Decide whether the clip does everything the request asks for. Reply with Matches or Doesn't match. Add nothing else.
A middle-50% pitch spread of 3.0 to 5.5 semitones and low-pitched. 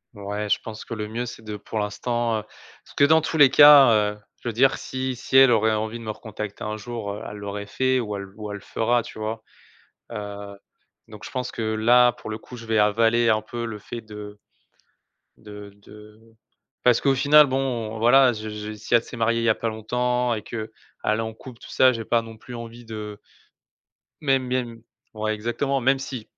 Doesn't match